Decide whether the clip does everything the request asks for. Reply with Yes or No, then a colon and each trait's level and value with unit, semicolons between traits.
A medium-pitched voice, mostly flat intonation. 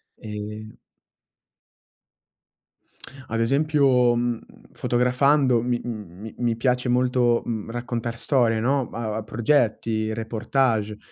No: low, 120 Hz; narrow, 2.1 semitones